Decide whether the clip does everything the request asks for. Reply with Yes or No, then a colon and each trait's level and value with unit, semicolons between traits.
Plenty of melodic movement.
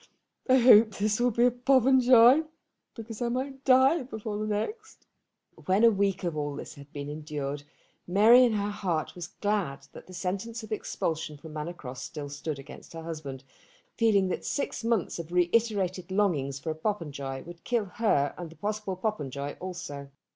Yes: wide, 6.8 semitones